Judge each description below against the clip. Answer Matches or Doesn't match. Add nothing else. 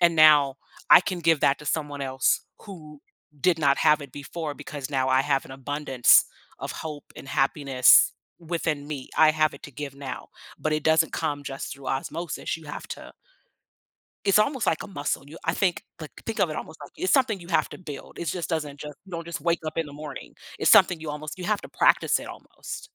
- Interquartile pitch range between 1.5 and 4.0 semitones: Matches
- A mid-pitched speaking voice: Matches